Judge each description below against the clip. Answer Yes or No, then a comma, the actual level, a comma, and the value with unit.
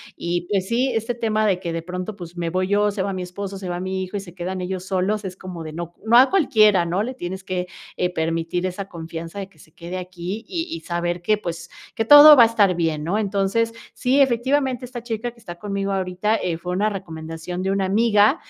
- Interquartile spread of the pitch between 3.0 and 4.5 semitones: Yes, average, 3.5 semitones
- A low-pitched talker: No, high, 190 Hz